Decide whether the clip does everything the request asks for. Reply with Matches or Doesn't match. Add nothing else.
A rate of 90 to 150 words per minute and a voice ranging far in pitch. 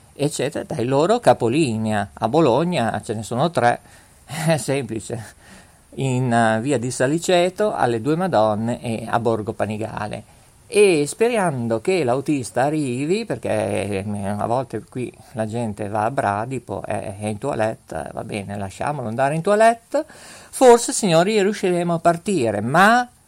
Matches